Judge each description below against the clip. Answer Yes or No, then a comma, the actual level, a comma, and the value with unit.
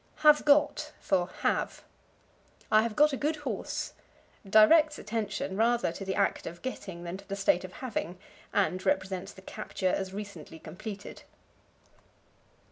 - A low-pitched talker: No, high, 200 Hz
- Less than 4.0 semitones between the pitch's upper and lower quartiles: No, average, 4.9 semitones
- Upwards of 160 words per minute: No, average, 145 wpm